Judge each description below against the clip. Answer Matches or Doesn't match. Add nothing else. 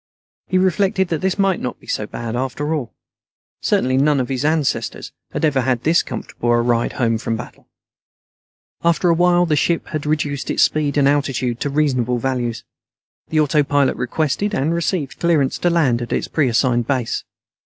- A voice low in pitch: Doesn't match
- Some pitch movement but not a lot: Matches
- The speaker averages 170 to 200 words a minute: Matches